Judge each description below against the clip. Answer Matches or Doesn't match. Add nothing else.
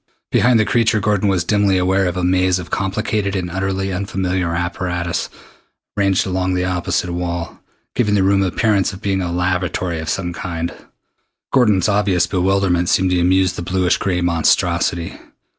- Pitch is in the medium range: Doesn't match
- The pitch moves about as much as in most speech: Doesn't match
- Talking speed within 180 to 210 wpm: Doesn't match